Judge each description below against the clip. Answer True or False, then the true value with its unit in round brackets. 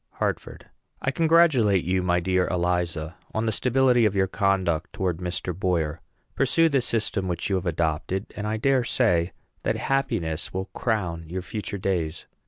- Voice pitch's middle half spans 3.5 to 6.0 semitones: True (4.3 semitones)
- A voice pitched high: False (95 Hz)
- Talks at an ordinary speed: True (165 wpm)